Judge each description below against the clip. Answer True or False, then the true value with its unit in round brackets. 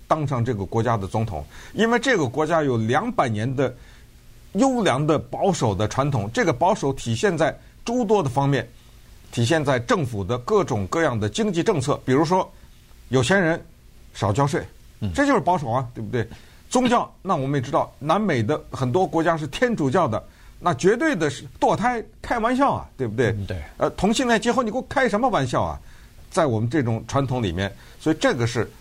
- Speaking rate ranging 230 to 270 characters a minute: False (285 characters per minute)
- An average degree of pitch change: False (8.5 semitones)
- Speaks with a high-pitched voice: False (140 Hz)